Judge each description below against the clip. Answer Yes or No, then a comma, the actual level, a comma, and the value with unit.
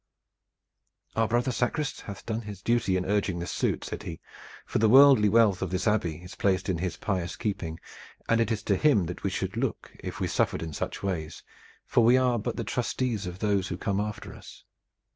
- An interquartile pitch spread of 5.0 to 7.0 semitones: No, average, 4.0 semitones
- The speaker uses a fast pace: Yes, fast, 210 wpm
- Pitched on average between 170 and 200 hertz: No, low, 105 Hz